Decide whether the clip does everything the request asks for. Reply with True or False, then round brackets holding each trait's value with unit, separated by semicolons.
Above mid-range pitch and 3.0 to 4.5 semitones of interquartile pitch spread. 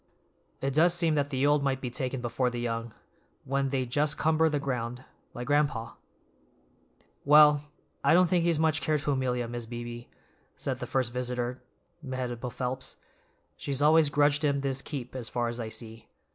False (135 Hz; 3.3 semitones)